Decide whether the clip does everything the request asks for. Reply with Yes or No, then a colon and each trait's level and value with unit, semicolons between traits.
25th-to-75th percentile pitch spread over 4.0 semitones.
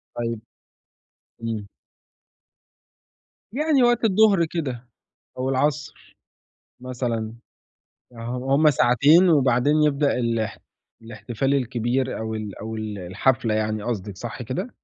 Yes: average, 4.5 semitones